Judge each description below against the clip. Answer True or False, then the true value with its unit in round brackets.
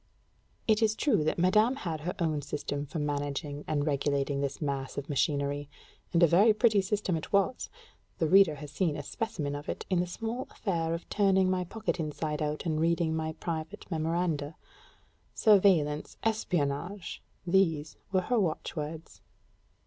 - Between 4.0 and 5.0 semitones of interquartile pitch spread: True (4.5 semitones)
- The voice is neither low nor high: True (165 Hz)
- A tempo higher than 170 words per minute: False (160 wpm)